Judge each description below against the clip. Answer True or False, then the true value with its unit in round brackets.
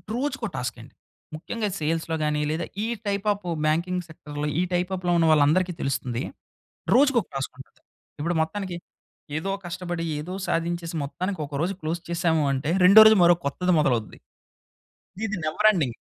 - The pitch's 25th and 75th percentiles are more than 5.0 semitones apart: False (3.6 semitones)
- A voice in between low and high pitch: True (170 Hz)